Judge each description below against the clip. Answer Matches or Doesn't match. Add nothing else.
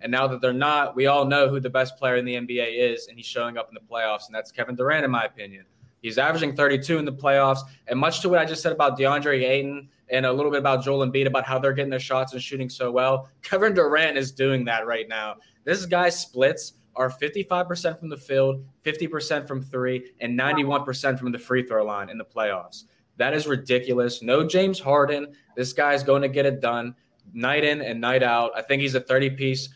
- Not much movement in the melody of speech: Matches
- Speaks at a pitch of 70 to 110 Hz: Doesn't match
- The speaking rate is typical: Doesn't match